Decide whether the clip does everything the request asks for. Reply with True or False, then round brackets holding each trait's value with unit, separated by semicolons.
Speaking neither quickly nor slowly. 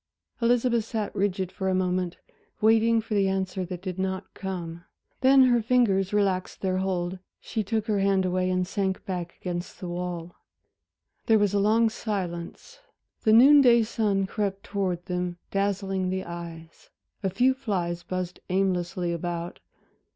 True (155 wpm)